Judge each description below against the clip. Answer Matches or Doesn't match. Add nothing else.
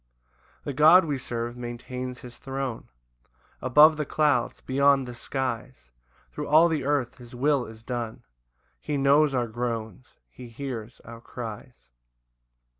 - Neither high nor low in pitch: Doesn't match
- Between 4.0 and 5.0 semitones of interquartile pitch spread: Doesn't match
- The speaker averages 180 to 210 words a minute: Doesn't match